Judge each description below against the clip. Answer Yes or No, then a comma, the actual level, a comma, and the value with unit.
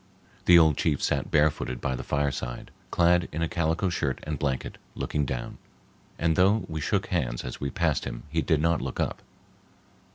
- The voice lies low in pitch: Yes, very low, 80 Hz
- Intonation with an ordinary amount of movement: Yes, average, 3.5 semitones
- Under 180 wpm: No, average, 185 wpm